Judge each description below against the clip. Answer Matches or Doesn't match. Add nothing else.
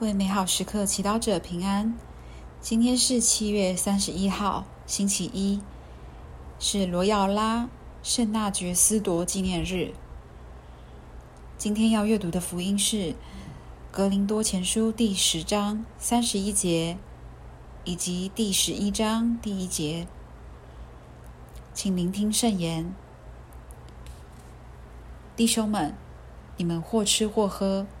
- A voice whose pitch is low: Doesn't match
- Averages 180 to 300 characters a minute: Doesn't match